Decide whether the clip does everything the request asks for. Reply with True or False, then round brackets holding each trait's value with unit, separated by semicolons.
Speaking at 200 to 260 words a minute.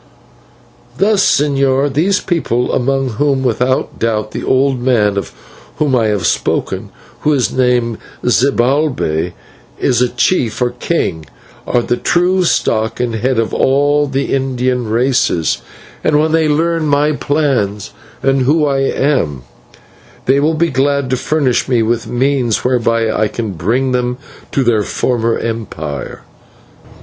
False (140 wpm)